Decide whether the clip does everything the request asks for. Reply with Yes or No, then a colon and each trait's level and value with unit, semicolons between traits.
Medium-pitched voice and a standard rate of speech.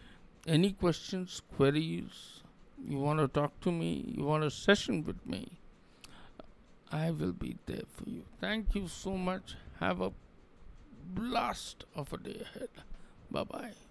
Yes: medium, 155 Hz; average, 145 wpm